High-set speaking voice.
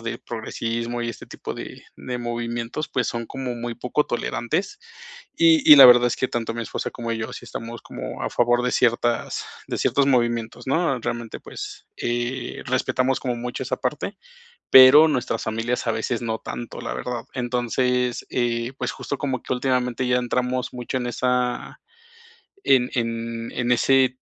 No: low, 120 Hz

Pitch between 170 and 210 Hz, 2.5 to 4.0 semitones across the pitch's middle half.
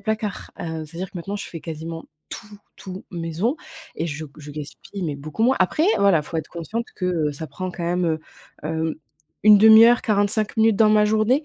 No: medium, 185 Hz; average, 5.0 semitones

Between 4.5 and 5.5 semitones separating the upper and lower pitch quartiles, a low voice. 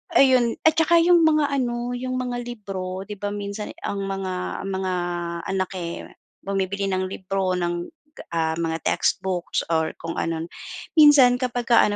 No: average, 5.0 semitones; high, 200 Hz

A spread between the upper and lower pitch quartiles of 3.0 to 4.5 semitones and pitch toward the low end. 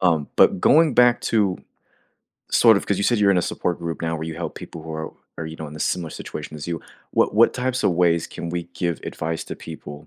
Yes: average, 4.0 semitones; very low, 85 Hz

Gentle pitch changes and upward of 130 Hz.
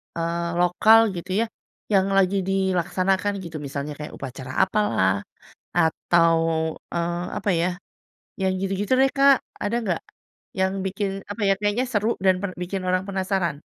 No: average, 3.0 semitones; high, 190 Hz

